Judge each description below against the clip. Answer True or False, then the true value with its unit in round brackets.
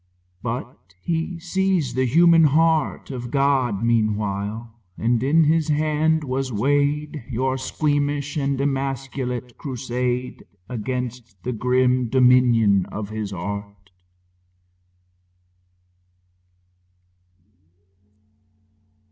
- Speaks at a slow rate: True (85 wpm)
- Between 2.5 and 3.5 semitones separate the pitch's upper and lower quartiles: False (3.9 semitones)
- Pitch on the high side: False (130 Hz)